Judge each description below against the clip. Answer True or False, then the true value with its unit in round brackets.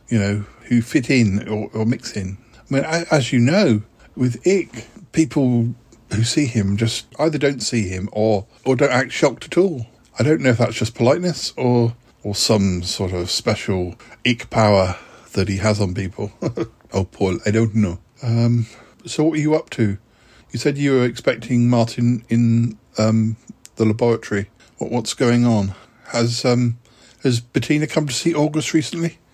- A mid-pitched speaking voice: False (115 Hz)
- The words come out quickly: False (180 wpm)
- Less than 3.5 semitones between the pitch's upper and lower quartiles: True (2.8 semitones)